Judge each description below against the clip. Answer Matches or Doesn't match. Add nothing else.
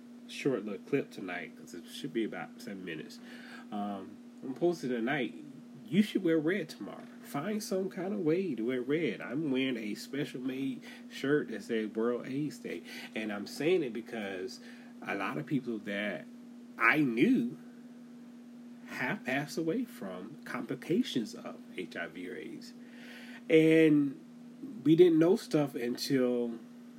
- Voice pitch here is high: Matches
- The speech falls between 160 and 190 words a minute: Doesn't match